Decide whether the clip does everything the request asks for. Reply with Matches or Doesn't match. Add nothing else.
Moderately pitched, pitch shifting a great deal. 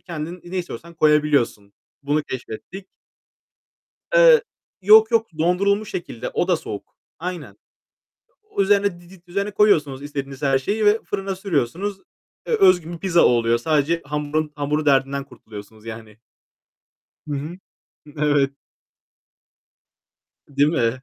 Matches